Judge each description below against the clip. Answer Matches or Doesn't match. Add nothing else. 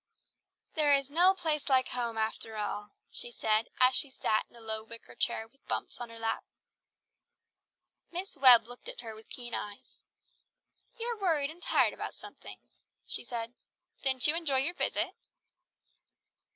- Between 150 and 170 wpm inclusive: Matches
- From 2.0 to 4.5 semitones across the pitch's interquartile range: Doesn't match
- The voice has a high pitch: Matches